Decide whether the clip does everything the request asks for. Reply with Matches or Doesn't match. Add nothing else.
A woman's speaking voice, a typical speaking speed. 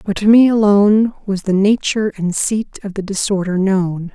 Matches